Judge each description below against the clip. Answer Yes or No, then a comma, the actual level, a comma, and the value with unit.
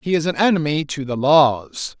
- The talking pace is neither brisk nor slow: No, fast, 210 wpm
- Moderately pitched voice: Yes, medium, 150 Hz